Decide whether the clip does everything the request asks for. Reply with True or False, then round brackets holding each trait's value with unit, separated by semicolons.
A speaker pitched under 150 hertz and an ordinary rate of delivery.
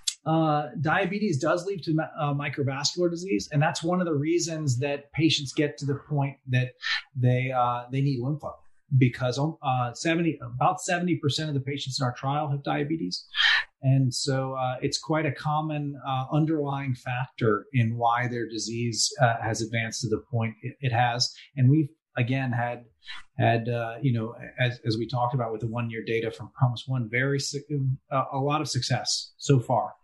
True (135 Hz; 180 wpm)